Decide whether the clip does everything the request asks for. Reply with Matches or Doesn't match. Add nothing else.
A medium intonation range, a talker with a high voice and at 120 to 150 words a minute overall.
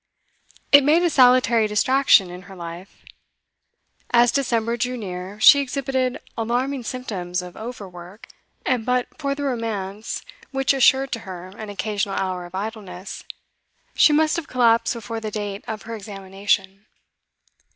Matches